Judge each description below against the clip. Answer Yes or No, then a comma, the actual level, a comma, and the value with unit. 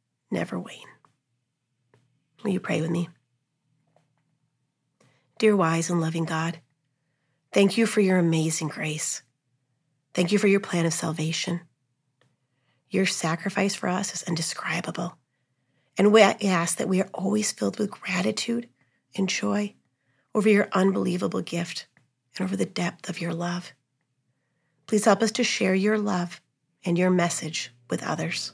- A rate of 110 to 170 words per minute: Yes, average, 140 wpm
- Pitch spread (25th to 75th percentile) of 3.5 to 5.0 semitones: No, wide, 5.4 semitones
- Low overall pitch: No, medium, 165 Hz